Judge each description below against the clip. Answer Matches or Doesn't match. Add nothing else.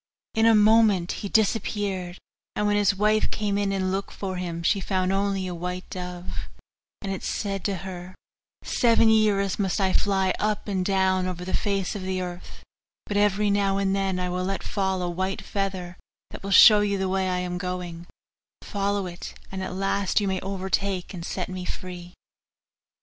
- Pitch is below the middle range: Doesn't match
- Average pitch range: Doesn't match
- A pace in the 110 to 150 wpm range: Doesn't match